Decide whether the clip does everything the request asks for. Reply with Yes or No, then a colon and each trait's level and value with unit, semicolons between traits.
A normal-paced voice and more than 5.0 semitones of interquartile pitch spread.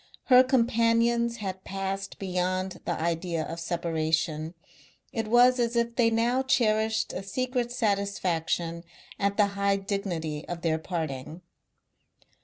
No: slow, 125 wpm; wide, 5.5 semitones